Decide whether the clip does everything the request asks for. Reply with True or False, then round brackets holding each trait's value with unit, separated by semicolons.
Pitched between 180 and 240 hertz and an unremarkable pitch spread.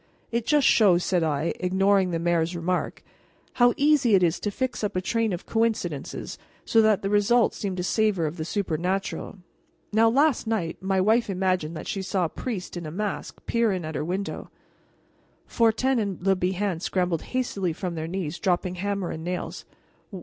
True (190 Hz; 3.9 semitones)